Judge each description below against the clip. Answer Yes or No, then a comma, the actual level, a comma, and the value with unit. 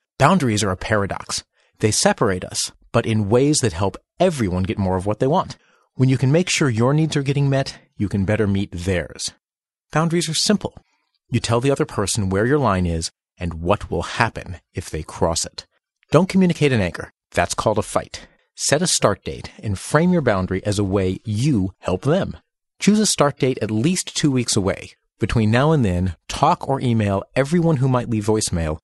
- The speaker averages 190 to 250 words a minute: Yes, average, 200 wpm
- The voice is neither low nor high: No, low, 115 Hz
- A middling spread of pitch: No, wide, 6.8 semitones